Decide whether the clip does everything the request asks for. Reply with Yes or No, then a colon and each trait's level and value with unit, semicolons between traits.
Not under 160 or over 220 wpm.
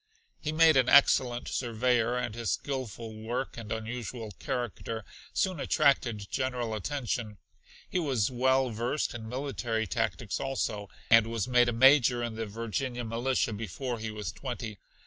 No: average, 145 wpm